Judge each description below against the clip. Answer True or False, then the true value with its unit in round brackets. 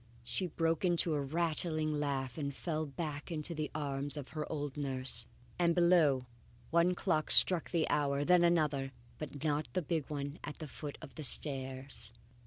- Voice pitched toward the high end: False (150 Hz)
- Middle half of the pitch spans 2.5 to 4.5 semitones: True (2.9 semitones)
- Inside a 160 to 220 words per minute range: True (180 wpm)